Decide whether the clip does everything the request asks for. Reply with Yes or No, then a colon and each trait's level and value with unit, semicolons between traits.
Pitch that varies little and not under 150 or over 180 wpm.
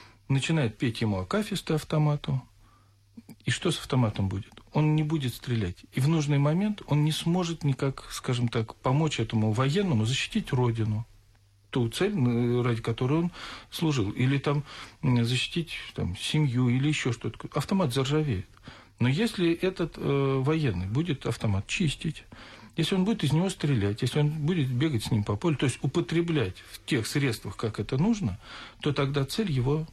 No: wide, 5.5 semitones; fast, 160 wpm